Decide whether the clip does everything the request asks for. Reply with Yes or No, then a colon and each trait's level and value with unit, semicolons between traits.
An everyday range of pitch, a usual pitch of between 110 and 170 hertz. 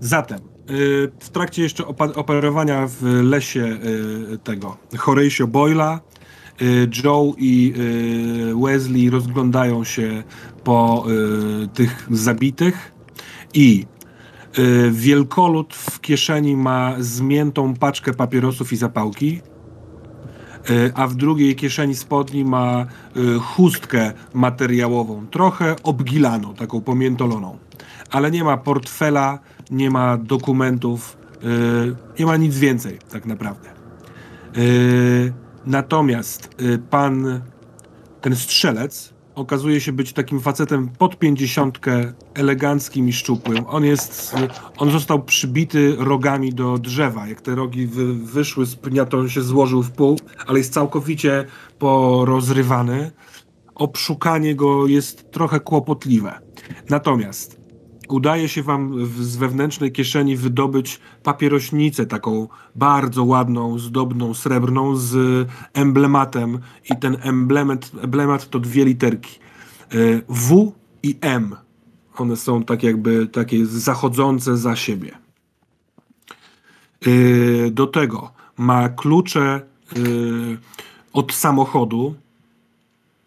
Yes: average, 3.0 semitones; low, 130 Hz